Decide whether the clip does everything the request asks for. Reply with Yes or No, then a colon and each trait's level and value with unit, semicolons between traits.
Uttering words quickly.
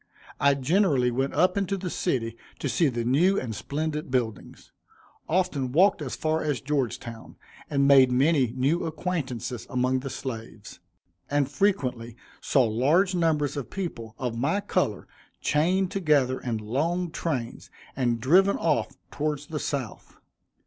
No: average, 140 wpm